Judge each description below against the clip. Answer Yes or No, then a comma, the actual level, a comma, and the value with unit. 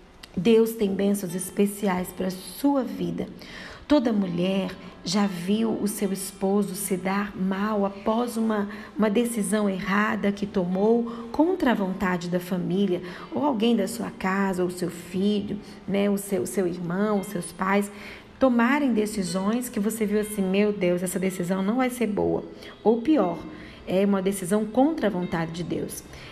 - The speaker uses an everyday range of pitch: No, narrow, 2.3 semitones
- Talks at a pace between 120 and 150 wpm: No, average, 160 wpm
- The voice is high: Yes, high, 200 Hz